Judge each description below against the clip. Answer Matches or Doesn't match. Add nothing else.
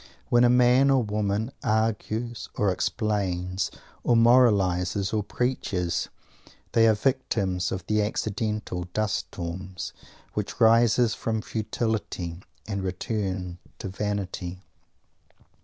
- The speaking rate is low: Matches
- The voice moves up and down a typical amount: Matches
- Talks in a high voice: Doesn't match